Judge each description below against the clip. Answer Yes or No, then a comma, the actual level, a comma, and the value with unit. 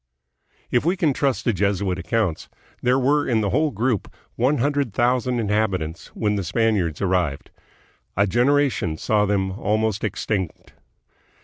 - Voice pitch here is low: Yes, low, 110 Hz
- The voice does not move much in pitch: No, average, 4.7 semitones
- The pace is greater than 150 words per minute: No, average, 145 wpm